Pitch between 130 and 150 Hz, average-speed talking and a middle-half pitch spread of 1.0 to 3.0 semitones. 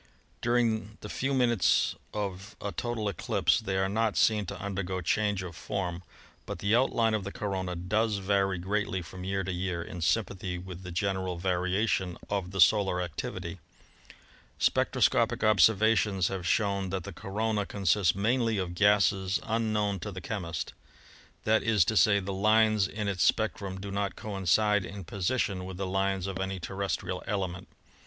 No: low, 100 Hz; average, 160 wpm; narrow, 2.4 semitones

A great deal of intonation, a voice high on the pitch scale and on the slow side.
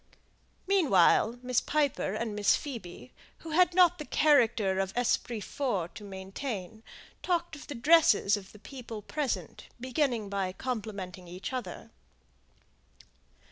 Yes: wide, 6.6 semitones; high, 230 Hz; slow, 130 wpm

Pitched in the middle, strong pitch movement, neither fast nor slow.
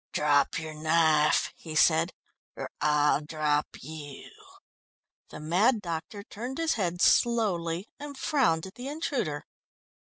No: medium, 165 Hz; wide, 6.6 semitones; slow, 125 wpm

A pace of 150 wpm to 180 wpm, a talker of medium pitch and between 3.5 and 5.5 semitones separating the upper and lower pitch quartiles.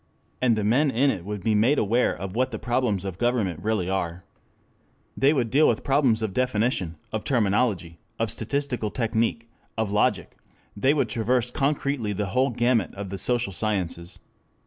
No: average, 170 wpm; low, 110 Hz; average, 4.1 semitones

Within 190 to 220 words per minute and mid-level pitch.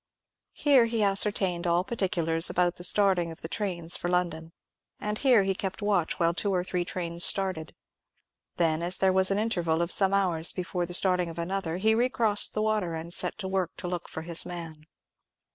Yes: average, 200 wpm; medium, 180 Hz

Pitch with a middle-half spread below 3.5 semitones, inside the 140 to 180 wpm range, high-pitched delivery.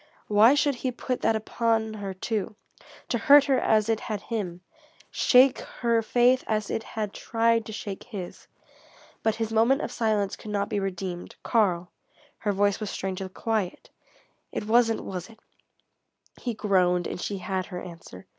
Yes: average, 3.0 semitones; average, 165 wpm; high, 215 Hz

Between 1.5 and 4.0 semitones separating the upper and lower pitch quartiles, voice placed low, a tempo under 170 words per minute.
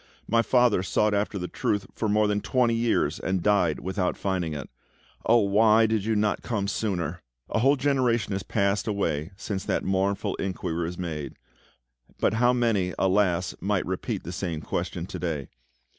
No: average, 3.5 semitones; low, 100 Hz; average, 175 wpm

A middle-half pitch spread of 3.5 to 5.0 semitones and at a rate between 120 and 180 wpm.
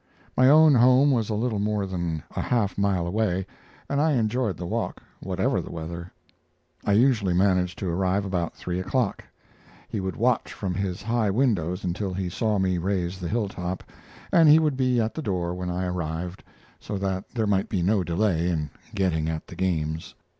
No: average, 3.9 semitones; average, 190 wpm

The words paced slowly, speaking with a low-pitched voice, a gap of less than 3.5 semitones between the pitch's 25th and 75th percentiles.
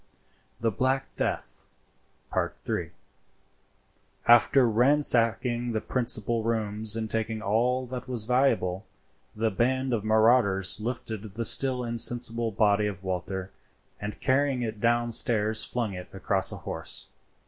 Yes: slow, 115 wpm; low, 115 Hz; average, 2.7 semitones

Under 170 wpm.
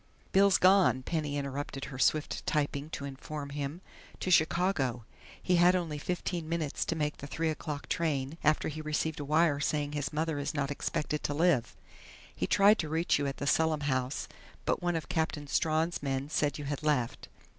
No: average, 190 wpm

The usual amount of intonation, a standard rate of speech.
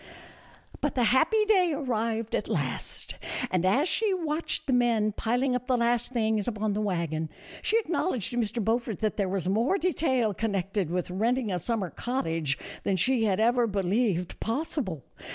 Yes: average, 4.7 semitones; average, 170 wpm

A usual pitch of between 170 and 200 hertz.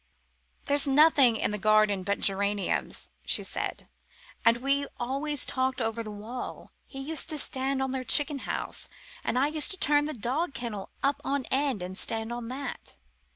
No: very high, 260 Hz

